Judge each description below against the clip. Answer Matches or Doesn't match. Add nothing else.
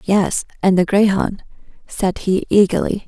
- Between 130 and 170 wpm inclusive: Matches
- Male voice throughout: Doesn't match